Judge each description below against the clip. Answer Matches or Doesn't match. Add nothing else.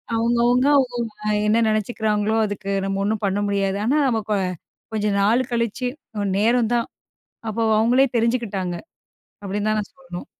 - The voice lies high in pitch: Matches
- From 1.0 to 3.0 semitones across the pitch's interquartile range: Matches